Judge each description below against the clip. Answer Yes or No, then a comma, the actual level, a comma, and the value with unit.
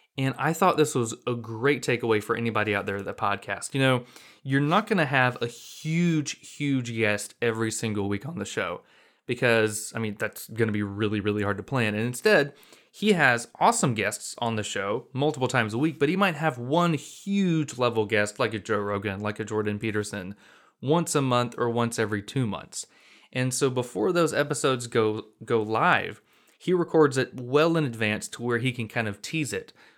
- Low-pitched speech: Yes, low, 120 Hz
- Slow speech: No, fast, 205 wpm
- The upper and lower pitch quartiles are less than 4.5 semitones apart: No, average, 5.2 semitones